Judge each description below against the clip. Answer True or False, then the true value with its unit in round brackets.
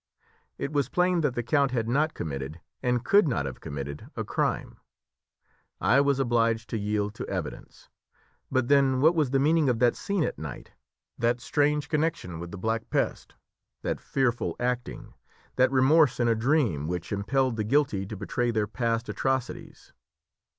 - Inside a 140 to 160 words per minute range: False (170 wpm)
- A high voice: False (125 Hz)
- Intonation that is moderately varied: True (4.7 semitones)